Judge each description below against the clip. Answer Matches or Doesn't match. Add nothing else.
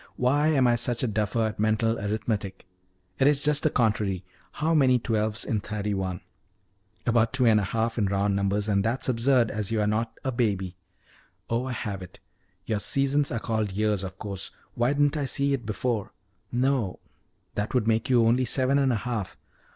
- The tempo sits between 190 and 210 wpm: Matches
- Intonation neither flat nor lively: Matches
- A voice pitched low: Matches